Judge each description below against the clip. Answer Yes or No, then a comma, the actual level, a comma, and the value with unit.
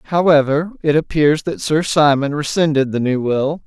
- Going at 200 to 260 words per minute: No, average, 165 wpm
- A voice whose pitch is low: No, medium, 150 Hz